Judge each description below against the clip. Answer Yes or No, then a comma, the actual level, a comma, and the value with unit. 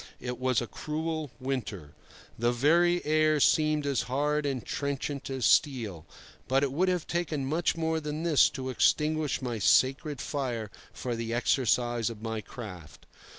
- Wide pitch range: No, average, 4.3 semitones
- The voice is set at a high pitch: No, low, 135 Hz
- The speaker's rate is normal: Yes, average, 155 wpm